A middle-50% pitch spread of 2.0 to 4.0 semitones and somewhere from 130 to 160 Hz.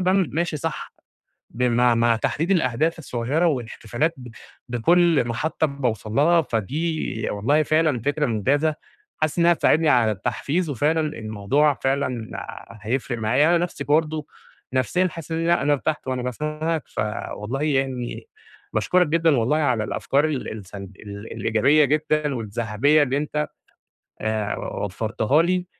No: average, 5.1 semitones; medium, 140 Hz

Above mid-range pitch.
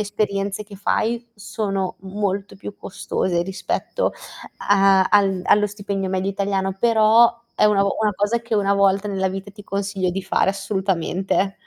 Yes: high, 200 Hz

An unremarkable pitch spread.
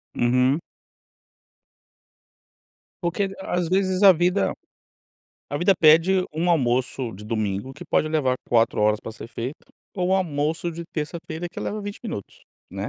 No: wide, 6.1 semitones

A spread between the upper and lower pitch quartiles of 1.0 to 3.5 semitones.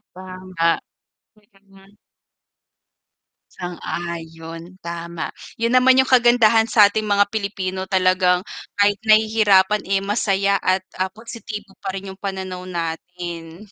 Yes: average, 2.8 semitones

